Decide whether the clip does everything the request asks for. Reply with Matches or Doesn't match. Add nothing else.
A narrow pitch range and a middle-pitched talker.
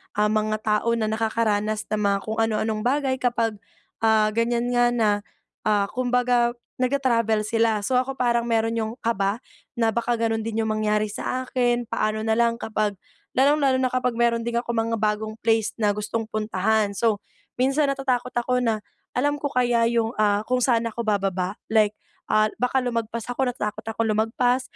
Doesn't match